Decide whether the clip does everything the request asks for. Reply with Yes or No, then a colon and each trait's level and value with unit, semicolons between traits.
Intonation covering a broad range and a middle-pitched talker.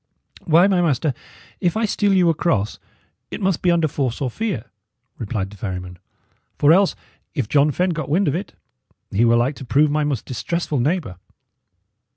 Yes: wide, 6.6 semitones; medium, 150 Hz